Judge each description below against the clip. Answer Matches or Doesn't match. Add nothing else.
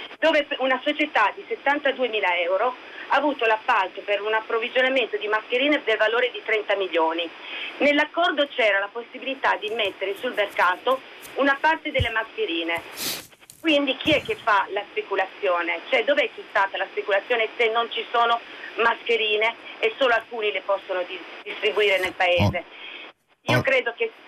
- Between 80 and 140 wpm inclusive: Doesn't match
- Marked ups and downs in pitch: Matches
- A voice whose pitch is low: Doesn't match